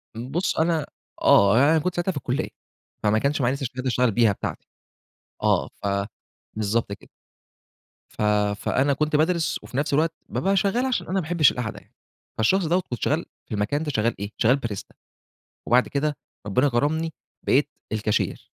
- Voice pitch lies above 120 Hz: Yes, medium, 140 Hz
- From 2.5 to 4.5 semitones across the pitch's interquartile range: No, wide, 5.6 semitones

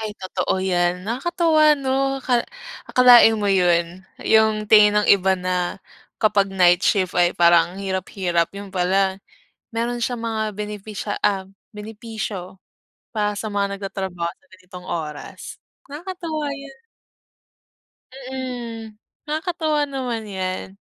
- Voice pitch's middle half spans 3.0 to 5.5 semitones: Yes, average, 4.5 semitones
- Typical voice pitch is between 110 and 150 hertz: No, high, 205 Hz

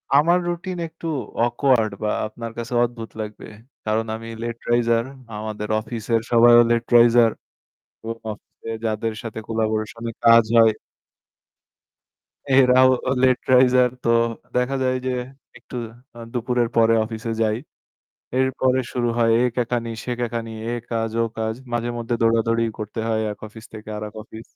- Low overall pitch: Yes, low, 115 Hz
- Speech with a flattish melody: Yes, narrow, 1.6 semitones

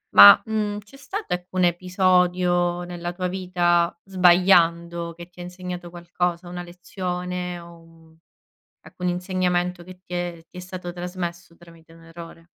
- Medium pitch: Yes, medium, 175 Hz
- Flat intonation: Yes, narrow, 1.0 semitones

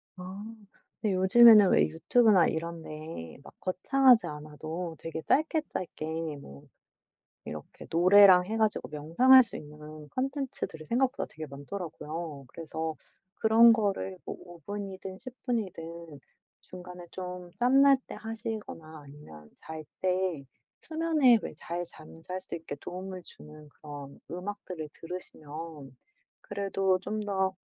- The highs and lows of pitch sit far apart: No, average, 5.0 semitones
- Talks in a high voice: No, medium, 180 Hz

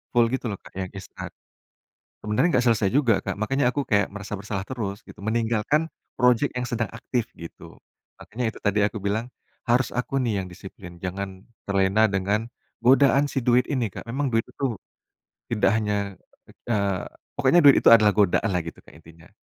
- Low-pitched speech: Yes, low, 110 Hz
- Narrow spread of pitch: No, average, 3.7 semitones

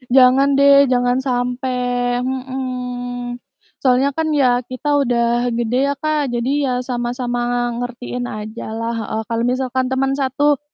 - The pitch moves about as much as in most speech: No, narrow, 1.4 semitones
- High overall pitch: Yes, very high, 250 Hz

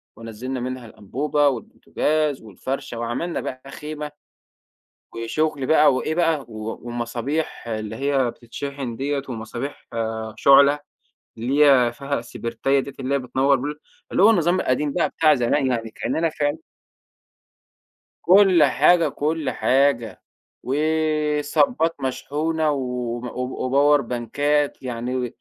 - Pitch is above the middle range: No, medium, 140 Hz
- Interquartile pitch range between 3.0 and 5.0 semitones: Yes, average, 3.8 semitones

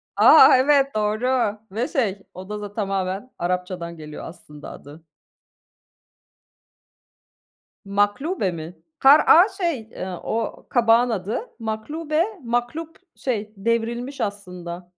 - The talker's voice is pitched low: No, high, 215 Hz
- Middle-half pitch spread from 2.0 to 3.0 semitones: No, average, 5.3 semitones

